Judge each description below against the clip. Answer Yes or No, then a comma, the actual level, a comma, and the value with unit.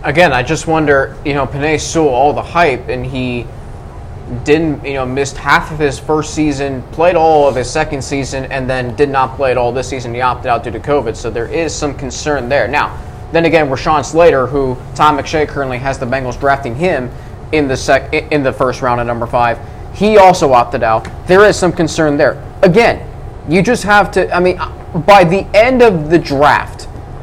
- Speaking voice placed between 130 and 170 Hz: Yes, medium, 140 Hz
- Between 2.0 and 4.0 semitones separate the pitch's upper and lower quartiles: No, average, 4.4 semitones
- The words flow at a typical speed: No, fast, 210 wpm